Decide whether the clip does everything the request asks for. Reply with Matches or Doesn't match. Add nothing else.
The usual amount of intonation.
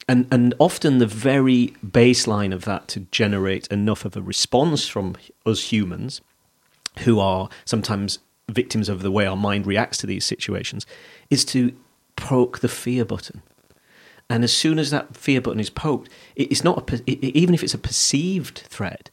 Matches